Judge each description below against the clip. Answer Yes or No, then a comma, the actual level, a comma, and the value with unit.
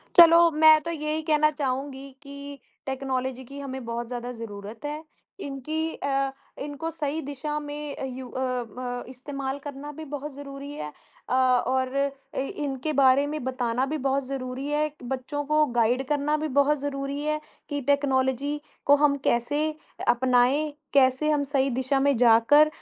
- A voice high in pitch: Yes, very high, 275 Hz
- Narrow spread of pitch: Yes, narrow, 2.3 semitones